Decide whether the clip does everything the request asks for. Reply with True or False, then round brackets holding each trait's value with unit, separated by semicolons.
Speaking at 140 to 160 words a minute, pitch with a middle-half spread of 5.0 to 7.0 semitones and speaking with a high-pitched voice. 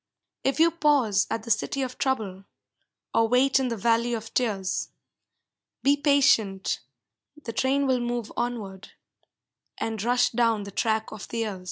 False (155 wpm; 3.4 semitones; 235 Hz)